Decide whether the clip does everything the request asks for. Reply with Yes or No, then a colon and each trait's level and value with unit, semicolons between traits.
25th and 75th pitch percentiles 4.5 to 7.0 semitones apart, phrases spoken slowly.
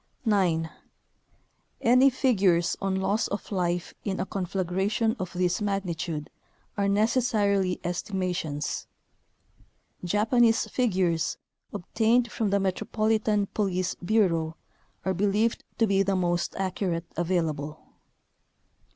No: average, 3.3 semitones; slow, 110 wpm